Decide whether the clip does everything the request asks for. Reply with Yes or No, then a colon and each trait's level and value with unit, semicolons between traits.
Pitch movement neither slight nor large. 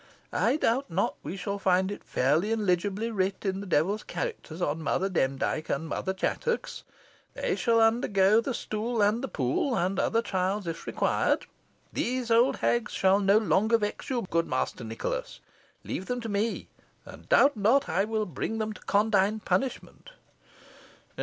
Yes: average, 3.5 semitones